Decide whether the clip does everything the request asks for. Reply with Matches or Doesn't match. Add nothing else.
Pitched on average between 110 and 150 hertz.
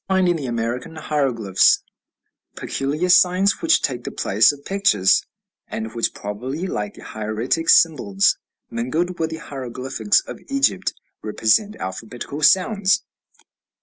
Matches